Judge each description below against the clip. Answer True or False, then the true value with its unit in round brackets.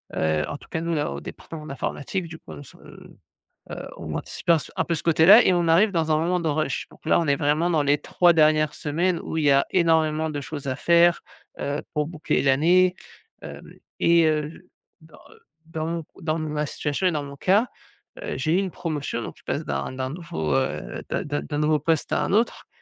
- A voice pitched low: False (155 Hz)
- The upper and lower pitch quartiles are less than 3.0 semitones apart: True (2.6 semitones)